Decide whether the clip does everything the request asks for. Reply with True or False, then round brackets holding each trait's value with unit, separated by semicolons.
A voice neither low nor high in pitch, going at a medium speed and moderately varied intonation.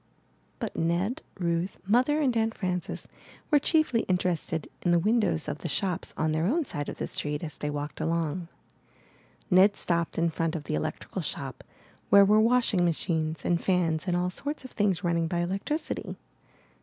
True (175 Hz; 175 wpm; 4.2 semitones)